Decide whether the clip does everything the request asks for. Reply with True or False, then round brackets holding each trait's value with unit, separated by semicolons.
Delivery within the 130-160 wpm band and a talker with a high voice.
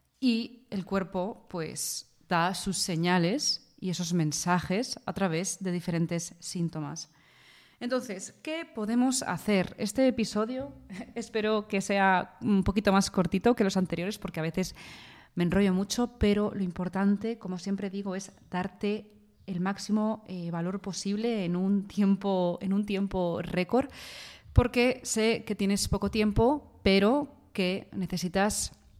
True (135 wpm; 195 Hz)